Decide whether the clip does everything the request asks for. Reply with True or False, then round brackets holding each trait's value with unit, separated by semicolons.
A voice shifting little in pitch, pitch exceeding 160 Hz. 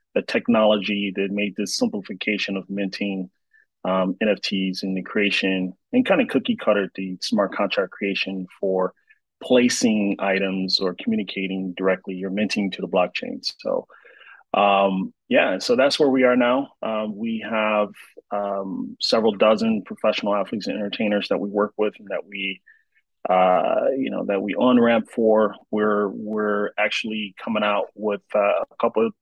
False (2.0 semitones; 100 Hz)